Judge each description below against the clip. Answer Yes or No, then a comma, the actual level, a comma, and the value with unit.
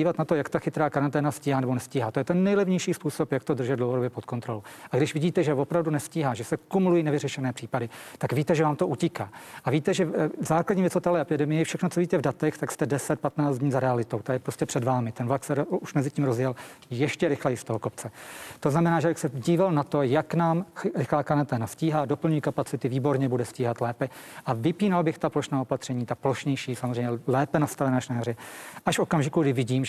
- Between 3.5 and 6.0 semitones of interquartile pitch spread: Yes, average, 3.9 semitones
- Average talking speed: No, fast, 220 wpm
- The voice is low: No, medium, 145 Hz